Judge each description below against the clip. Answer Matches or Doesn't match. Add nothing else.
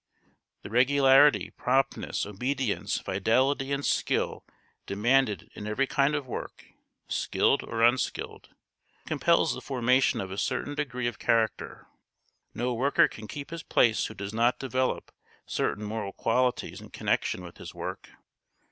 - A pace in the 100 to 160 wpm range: Matches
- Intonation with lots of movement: Doesn't match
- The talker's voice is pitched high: Doesn't match